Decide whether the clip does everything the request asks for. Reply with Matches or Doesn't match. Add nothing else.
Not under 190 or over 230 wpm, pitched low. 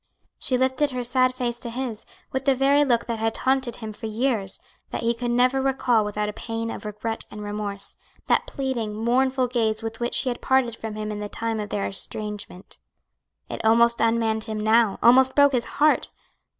Doesn't match